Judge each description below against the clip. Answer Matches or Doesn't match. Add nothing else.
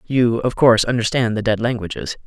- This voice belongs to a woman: Doesn't match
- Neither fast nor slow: Matches